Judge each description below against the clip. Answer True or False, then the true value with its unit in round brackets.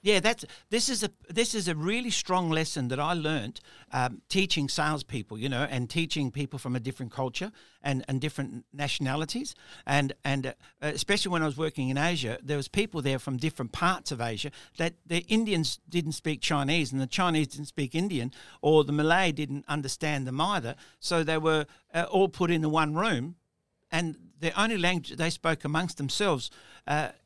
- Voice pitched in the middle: True (155 Hz)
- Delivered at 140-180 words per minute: False (190 wpm)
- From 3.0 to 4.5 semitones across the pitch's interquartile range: True (3.8 semitones)